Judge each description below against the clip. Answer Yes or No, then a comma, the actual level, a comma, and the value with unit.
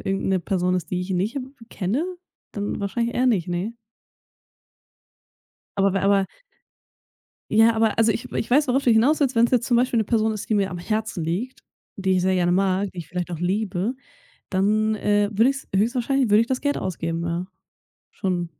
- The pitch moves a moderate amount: Yes, average, 4.0 semitones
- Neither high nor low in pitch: No, high, 205 Hz